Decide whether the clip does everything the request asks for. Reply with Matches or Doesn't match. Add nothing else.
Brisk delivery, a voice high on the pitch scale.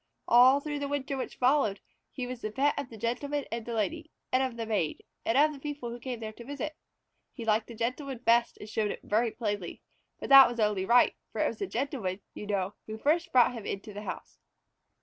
Matches